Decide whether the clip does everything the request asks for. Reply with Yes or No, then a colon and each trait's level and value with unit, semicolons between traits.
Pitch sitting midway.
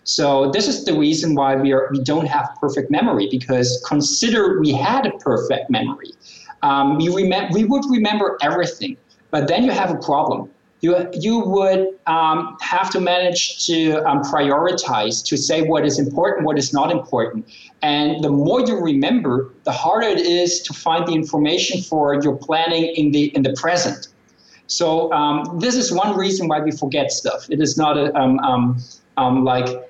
Yes: medium, 160 Hz